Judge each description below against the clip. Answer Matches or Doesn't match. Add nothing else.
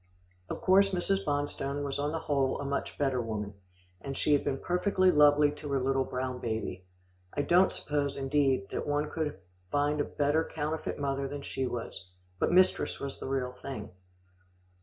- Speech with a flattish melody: Matches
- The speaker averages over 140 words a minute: Matches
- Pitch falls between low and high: Matches